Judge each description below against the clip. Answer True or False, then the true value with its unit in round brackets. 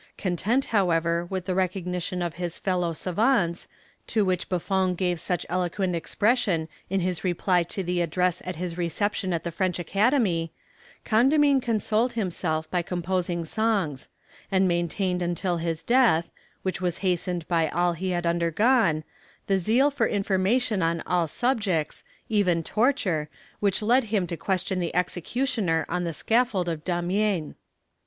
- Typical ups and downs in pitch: True (3.3 semitones)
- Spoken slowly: False (145 wpm)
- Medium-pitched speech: True (180 Hz)